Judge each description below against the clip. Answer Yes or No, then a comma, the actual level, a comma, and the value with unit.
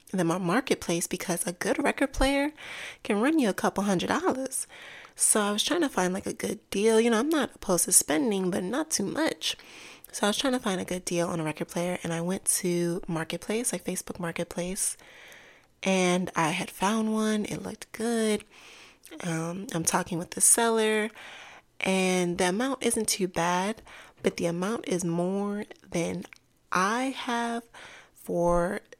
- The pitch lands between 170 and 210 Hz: Yes, high, 190 Hz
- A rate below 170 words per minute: No, average, 180 wpm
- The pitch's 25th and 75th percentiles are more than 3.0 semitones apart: Yes, average, 4.7 semitones